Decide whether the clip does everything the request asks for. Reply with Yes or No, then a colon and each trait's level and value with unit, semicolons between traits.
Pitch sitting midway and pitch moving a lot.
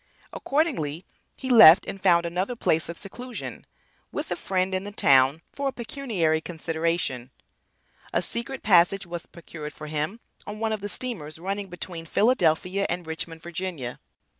No: medium, 180 Hz; average, 4.5 semitones